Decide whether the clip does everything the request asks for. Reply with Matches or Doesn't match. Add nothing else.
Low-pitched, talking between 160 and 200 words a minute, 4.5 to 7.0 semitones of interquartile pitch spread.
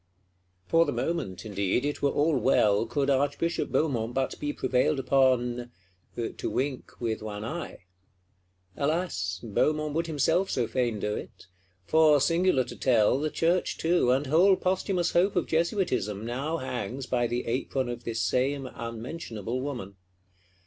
Doesn't match